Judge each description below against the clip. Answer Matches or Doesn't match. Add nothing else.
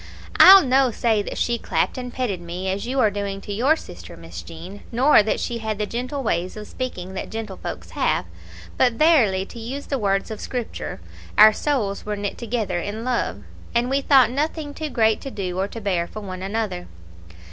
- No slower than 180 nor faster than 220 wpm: Matches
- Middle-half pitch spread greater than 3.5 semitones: Matches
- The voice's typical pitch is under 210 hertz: Doesn't match